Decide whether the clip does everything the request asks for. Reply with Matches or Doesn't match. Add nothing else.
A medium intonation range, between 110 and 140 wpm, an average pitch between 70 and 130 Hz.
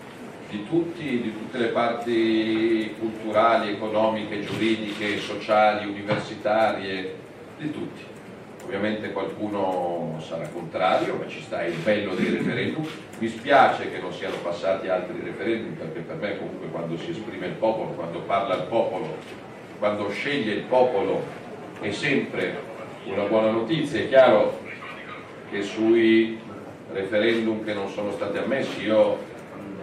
Doesn't match